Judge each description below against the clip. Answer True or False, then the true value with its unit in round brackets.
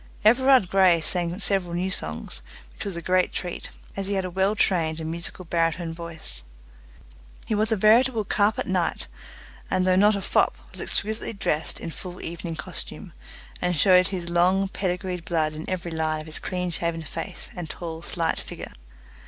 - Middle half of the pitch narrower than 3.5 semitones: True (2.6 semitones)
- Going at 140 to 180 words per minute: True (175 wpm)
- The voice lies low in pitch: False (180 Hz)